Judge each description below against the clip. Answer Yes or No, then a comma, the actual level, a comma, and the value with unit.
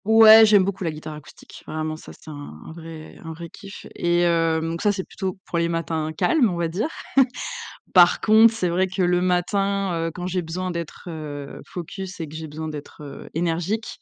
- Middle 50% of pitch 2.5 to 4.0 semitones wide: Yes, average, 2.9 semitones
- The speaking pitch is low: No, medium, 175 Hz